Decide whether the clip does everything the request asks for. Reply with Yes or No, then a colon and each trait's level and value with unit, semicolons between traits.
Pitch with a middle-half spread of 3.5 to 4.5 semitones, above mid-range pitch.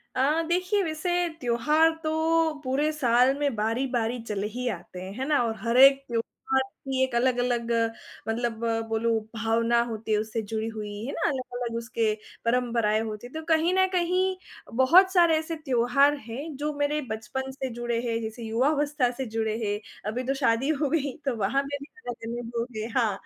Yes: average, 4.2 semitones; high, 245 Hz